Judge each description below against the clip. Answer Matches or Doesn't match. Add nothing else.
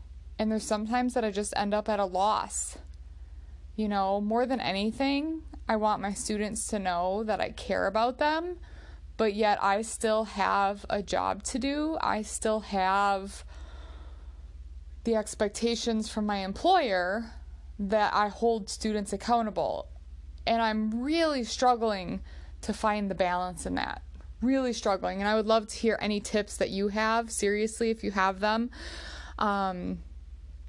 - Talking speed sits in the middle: Matches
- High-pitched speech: Matches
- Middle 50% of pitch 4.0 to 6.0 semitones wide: Doesn't match